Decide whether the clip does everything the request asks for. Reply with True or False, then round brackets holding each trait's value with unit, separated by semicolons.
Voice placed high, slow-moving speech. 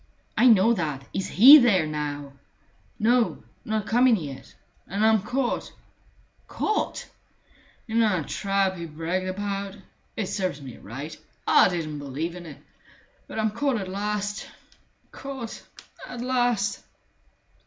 True (200 Hz; 130 wpm)